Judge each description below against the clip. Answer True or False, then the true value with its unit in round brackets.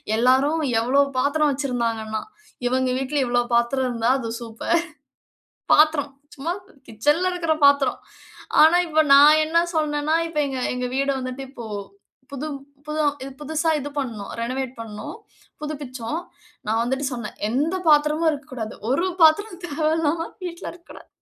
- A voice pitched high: True (280 Hz)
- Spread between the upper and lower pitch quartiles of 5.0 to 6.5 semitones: False (3.7 semitones)